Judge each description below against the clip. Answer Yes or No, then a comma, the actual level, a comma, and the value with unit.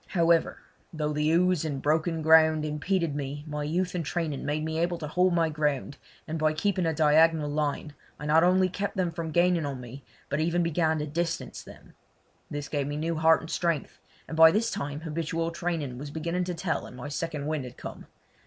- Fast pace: Yes, fast, 210 wpm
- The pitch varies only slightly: Yes, narrow, 2.2 semitones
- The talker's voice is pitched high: No, medium, 160 Hz